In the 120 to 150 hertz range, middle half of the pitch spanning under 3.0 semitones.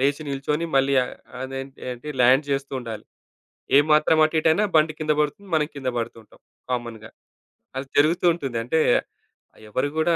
No: medium, 140 Hz; average, 3.3 semitones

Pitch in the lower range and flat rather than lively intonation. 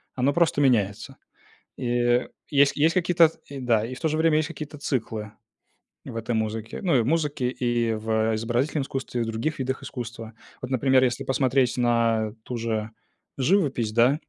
No: low, 125 Hz; average, 3.8 semitones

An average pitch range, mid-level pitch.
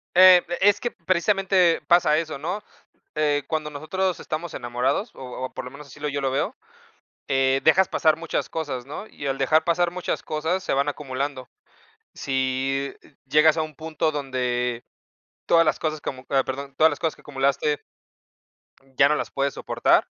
Yes: average, 3.5 semitones; medium, 150 Hz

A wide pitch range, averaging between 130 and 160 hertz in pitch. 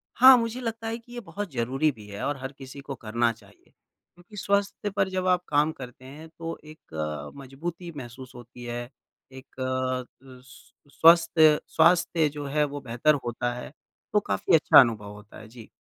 Yes: wide, 5.8 semitones; medium, 140 Hz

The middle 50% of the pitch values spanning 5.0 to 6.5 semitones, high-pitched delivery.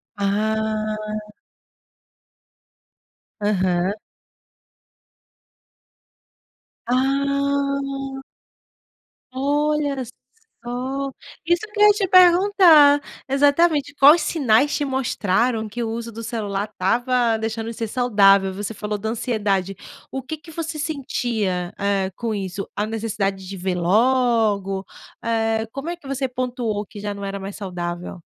Yes: wide, 5.5 semitones; high, 225 Hz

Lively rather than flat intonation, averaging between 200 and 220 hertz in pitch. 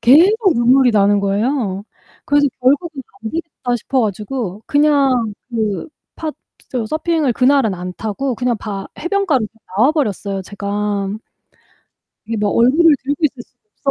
No: wide, 5.7 semitones; very high, 250 Hz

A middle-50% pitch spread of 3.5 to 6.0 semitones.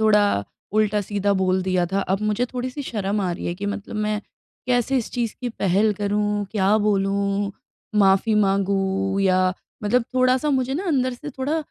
Yes: average, 3.9 semitones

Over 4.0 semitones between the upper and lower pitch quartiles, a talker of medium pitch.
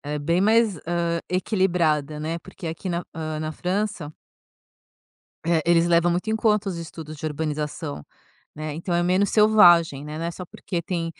No: average, 2.9 semitones; medium, 170 Hz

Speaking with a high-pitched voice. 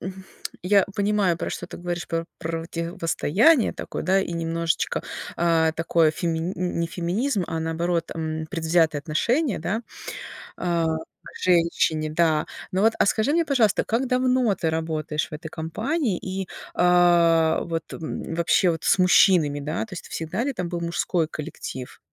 No: medium, 170 Hz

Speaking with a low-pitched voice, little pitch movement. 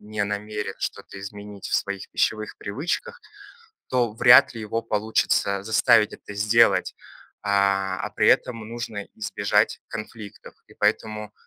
Yes: low, 105 Hz; narrow, 2.0 semitones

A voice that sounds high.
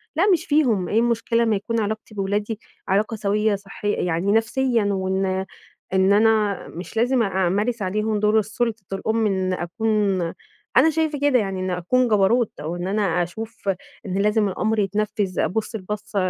Yes: high, 210 Hz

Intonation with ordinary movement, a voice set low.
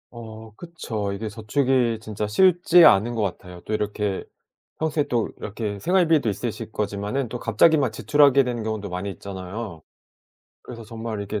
Yes: average, 3.8 semitones; low, 110 Hz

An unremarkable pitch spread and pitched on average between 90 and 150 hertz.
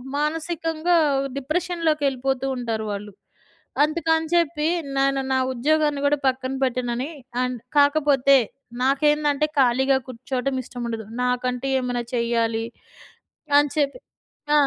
No: average, 3.4 semitones; very high, 275 Hz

